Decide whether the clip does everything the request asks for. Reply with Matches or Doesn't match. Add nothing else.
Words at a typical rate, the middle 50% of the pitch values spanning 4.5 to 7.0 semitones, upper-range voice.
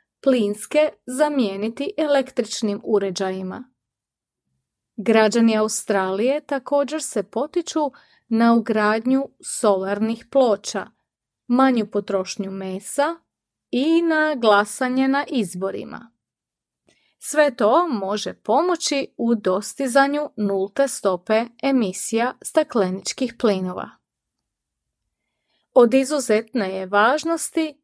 Doesn't match